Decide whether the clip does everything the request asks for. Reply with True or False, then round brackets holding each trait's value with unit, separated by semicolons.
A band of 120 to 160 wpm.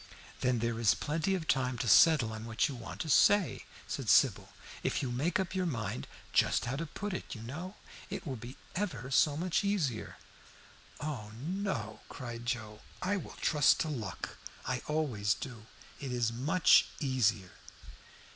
False (170 wpm)